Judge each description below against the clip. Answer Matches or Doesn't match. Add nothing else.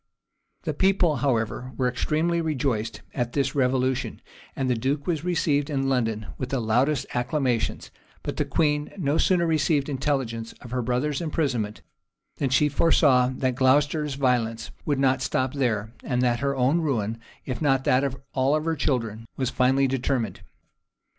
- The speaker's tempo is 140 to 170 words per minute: Matches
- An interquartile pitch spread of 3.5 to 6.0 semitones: Doesn't match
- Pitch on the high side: Doesn't match